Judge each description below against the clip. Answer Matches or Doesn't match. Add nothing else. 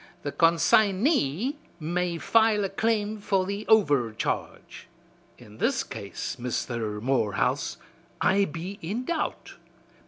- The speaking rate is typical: Doesn't match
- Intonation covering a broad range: Matches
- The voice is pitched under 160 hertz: Doesn't match